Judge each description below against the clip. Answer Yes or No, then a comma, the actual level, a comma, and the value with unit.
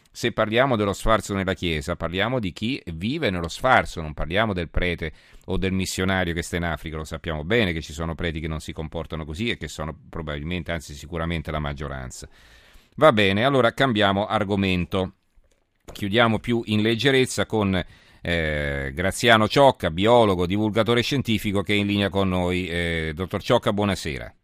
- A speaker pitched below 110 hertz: Yes, very low, 95 Hz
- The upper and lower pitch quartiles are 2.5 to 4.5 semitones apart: No, average, 4.9 semitones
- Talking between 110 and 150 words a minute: No, fast, 170 wpm